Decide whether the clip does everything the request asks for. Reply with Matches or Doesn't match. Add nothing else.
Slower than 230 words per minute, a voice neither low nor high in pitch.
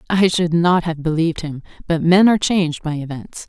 Matches